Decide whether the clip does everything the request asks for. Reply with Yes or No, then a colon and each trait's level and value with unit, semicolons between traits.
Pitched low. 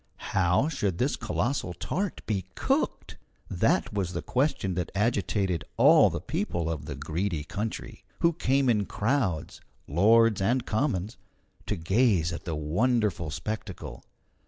Yes: low, 100 Hz